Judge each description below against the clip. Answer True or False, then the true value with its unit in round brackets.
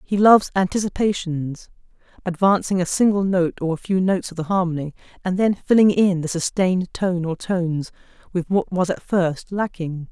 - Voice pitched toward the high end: False (180 Hz)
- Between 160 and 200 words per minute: True (165 wpm)